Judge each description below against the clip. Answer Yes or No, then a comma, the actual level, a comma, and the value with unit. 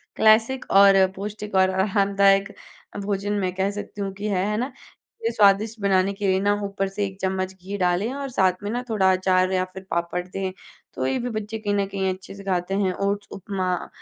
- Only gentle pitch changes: Yes, narrow, 1.5 semitones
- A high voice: Yes, high, 195 Hz